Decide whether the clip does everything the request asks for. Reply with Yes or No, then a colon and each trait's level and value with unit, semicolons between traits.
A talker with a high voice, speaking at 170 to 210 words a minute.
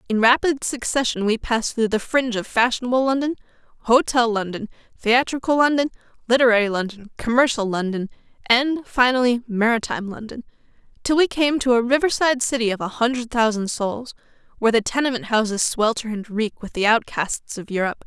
No: high, 235 Hz; average, 155 wpm